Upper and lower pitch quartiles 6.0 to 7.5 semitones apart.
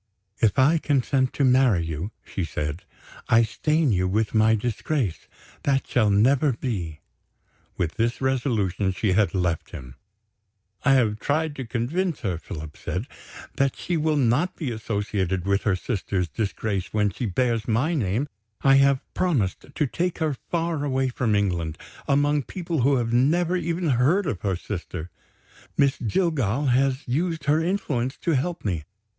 Yes: wide, 6.4 semitones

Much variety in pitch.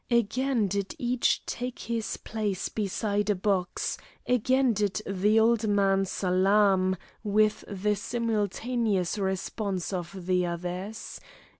No: average, 2.8 semitones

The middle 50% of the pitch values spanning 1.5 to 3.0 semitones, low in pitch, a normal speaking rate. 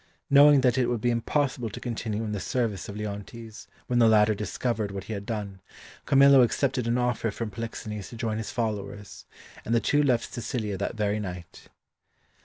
Yes: average, 2.7 semitones; low, 115 Hz; average, 190 wpm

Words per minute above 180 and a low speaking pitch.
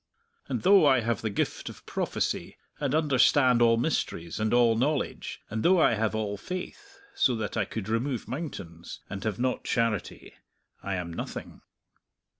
No: average, 170 wpm; low, 115 Hz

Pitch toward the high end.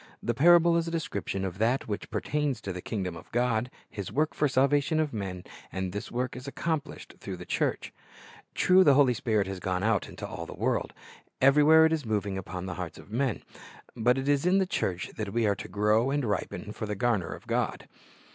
No: low, 120 Hz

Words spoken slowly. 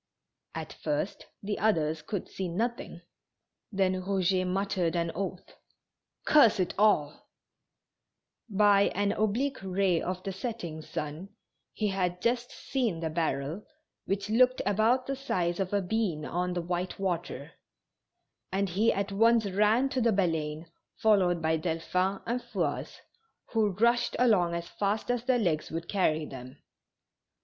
No: average, 145 wpm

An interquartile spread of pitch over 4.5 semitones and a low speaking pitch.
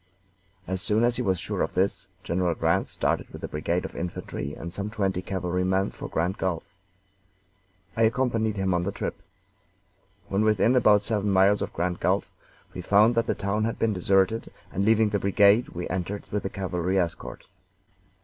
No: average, 2.8 semitones; very low, 95 Hz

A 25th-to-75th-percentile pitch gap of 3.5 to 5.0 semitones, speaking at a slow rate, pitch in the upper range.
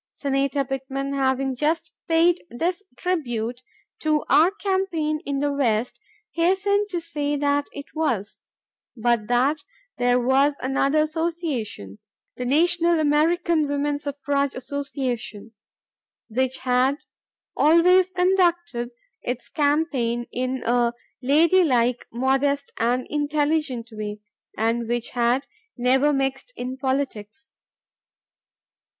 Yes: average, 4.0 semitones; slow, 105 wpm; very high, 280 Hz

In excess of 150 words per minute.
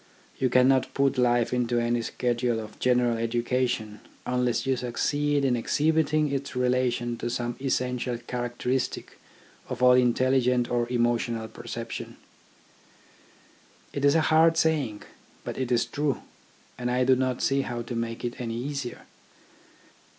No: average, 145 wpm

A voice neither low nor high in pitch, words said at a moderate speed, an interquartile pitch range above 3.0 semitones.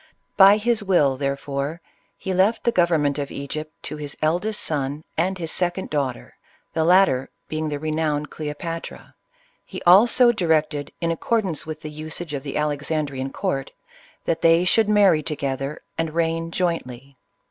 Yes: medium, 155 Hz; average, 160 wpm; average, 3.5 semitones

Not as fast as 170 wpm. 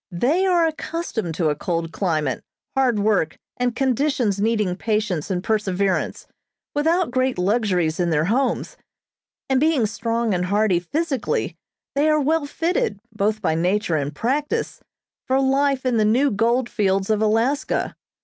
Yes: average, 150 wpm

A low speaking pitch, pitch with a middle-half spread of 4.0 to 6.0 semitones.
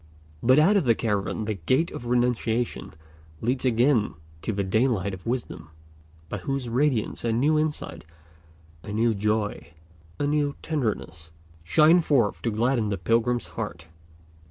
Yes: low, 115 Hz; average, 4.3 semitones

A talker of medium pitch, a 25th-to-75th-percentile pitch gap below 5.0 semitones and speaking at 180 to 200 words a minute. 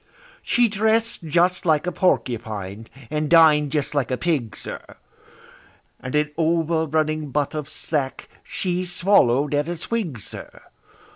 No: medium, 155 Hz; average, 3.7 semitones; average, 140 wpm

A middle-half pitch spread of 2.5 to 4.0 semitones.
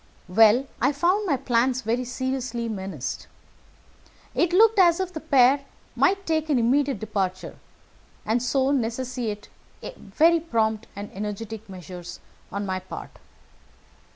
No: wide, 5.5 semitones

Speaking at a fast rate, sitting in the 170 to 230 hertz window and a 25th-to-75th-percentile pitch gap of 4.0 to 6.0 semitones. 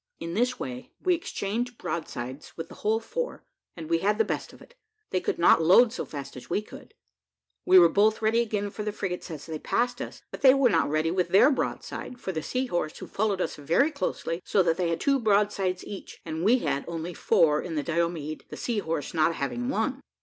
Yes: fast, 225 wpm; medium, 185 Hz; wide, 5.5 semitones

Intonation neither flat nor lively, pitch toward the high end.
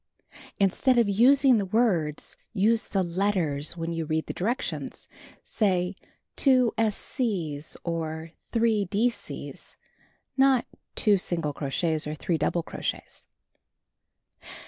No: wide, 5.8 semitones; high, 195 Hz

